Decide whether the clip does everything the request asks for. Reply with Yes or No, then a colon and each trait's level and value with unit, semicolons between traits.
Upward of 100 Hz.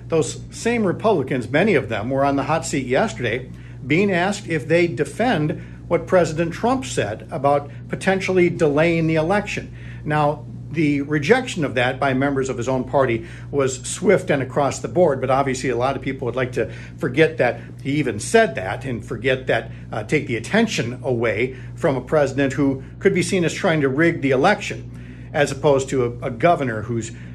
Yes: low, 135 Hz